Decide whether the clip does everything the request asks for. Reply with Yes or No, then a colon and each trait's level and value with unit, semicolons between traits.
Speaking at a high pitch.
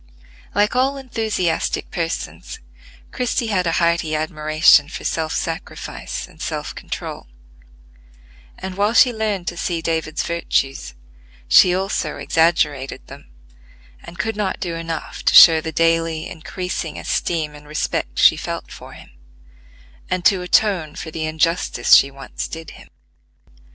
No: medium, 165 Hz